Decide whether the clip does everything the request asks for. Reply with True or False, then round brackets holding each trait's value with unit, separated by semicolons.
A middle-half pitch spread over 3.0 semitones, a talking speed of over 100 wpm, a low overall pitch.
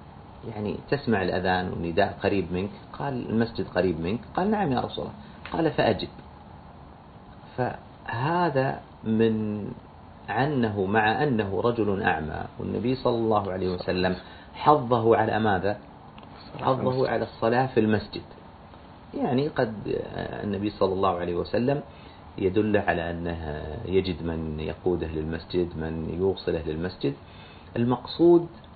True (5.2 semitones; 115 wpm; 100 Hz)